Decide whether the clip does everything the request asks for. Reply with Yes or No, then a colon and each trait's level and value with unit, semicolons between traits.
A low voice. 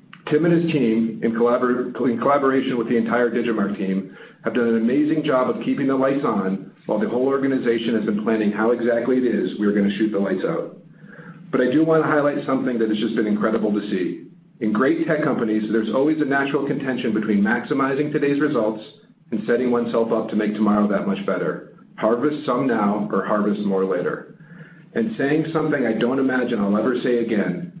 Yes: low, 120 Hz